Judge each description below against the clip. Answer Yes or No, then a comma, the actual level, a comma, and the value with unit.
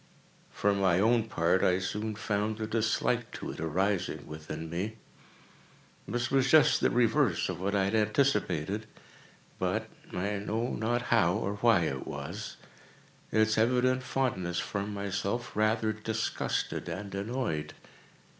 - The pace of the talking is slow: Yes, slow, 130 wpm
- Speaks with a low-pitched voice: Yes, low, 105 Hz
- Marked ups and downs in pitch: No, average, 3.2 semitones